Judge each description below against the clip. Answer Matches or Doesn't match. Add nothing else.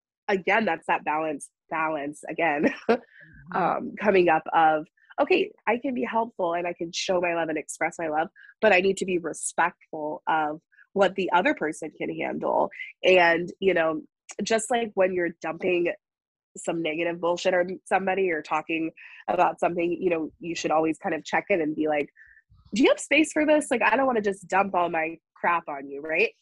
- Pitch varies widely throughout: Doesn't match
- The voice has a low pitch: Doesn't match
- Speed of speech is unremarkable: Matches